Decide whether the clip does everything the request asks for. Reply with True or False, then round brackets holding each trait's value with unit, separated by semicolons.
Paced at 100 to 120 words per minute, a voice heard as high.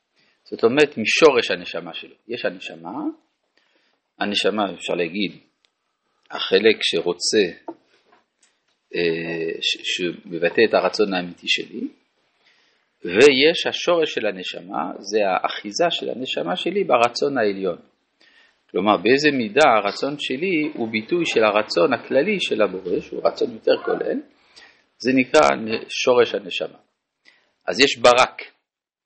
True (110 wpm; 335 Hz)